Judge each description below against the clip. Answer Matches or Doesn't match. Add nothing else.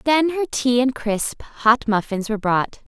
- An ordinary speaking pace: Matches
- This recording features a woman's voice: Matches